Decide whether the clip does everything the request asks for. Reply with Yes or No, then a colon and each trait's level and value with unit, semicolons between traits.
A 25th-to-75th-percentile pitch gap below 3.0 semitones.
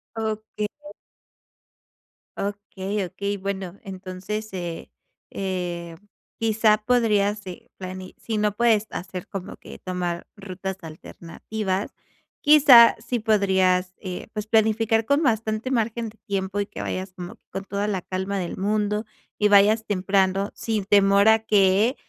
Yes: narrow, 2.6 semitones